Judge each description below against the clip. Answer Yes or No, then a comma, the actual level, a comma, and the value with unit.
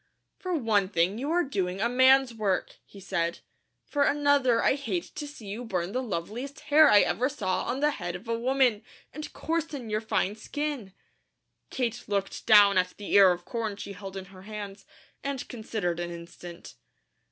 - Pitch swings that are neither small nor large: No, wide, 5.7 semitones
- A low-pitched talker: No, high, 220 Hz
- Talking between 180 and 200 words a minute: Yes, average, 185 wpm